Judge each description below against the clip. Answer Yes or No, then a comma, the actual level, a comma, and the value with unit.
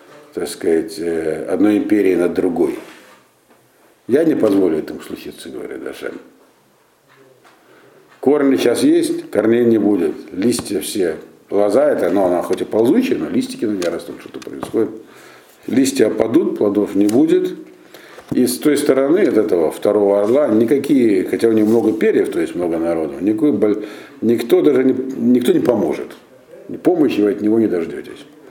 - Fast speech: No, average, 150 wpm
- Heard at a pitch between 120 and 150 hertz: Yes, low, 130 Hz